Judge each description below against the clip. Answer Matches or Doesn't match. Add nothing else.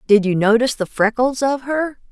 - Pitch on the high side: Matches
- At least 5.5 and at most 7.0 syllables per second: Doesn't match